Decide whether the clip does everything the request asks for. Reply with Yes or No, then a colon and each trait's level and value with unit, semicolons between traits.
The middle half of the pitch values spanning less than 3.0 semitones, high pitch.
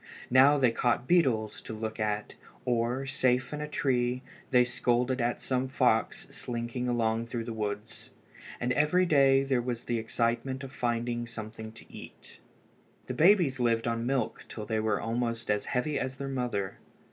No: narrow, 2.4 semitones; low, 120 Hz